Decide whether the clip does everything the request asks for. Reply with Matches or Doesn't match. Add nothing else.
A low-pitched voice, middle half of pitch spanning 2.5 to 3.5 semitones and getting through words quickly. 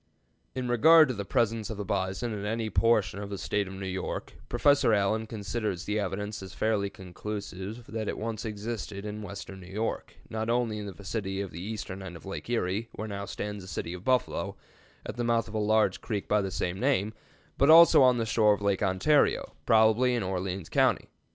Matches